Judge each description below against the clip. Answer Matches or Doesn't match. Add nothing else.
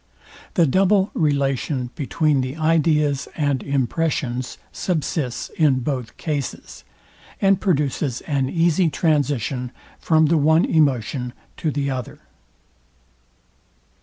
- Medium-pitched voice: Matches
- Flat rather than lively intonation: Doesn't match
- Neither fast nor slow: Doesn't match